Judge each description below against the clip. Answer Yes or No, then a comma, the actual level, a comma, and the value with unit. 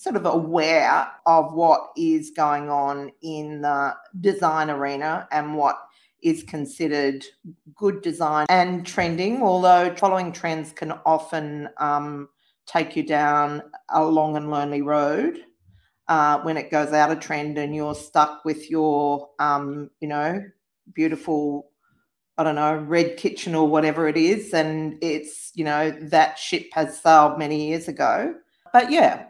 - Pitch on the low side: No, medium, 155 Hz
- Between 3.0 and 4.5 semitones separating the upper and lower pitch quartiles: No, narrow, 2.4 semitones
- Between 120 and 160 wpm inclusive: Yes, average, 145 wpm